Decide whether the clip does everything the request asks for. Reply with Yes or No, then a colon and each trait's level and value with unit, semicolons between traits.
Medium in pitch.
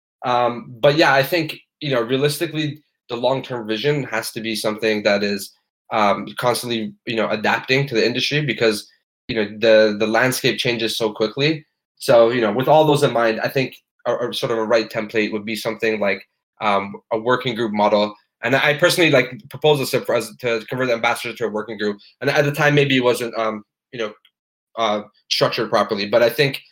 No: low, 120 Hz